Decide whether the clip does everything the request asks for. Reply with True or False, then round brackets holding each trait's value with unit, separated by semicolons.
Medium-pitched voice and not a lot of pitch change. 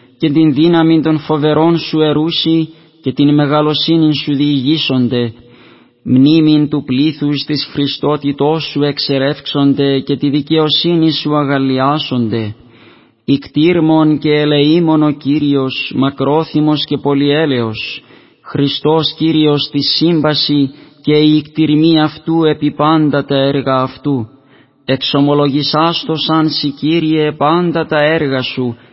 True (150 Hz; 2.1 semitones)